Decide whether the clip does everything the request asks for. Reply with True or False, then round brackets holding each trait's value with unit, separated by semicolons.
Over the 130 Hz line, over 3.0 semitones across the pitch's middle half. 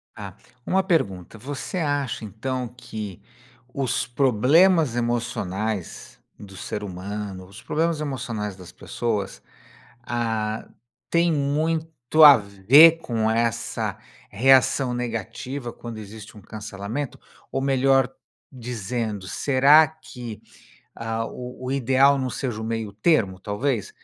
False (120 Hz; 4.5 semitones)